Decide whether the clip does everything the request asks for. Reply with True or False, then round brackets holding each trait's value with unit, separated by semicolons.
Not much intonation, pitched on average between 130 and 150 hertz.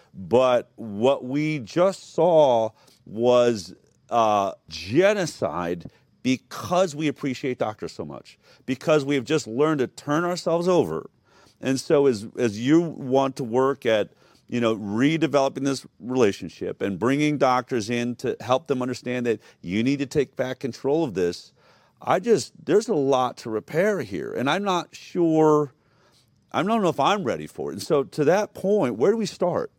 False (3.8 semitones; 135 Hz)